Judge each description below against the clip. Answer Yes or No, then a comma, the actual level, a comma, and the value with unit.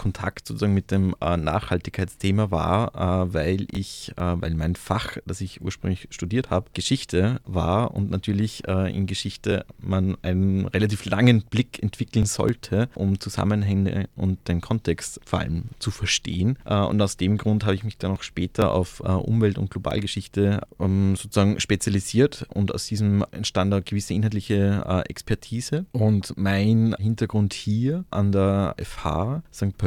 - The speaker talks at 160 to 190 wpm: No, average, 140 wpm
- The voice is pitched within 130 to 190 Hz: No, low, 100 Hz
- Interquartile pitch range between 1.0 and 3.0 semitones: Yes, narrow, 2.5 semitones